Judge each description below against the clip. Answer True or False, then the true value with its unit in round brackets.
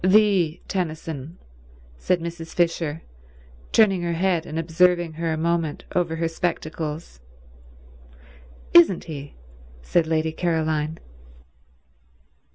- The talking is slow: True (100 wpm)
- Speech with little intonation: True (1.7 semitones)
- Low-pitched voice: False (165 Hz)